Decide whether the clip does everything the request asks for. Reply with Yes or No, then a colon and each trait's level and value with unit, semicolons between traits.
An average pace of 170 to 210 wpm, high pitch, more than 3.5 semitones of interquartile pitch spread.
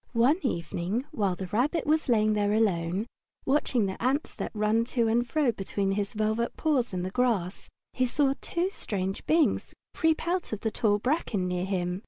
Yes: average, 185 wpm; high, 220 Hz; average, 5.3 semitones